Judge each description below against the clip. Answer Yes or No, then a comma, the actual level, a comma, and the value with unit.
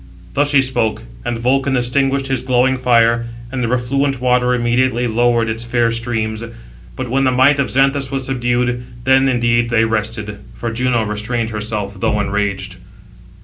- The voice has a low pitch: Yes, low, 120 Hz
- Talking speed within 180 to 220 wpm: No, average, 160 wpm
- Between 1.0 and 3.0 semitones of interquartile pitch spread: Yes, narrow, 2.4 semitones